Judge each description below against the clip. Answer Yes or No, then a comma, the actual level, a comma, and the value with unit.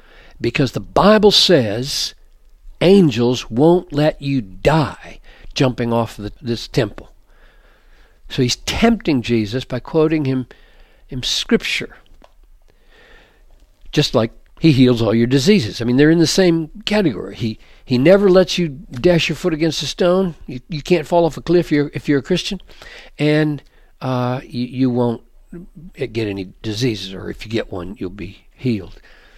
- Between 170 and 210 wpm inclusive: No, average, 155 wpm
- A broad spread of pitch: Yes, wide, 6.5 semitones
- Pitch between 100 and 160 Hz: Yes, low, 135 Hz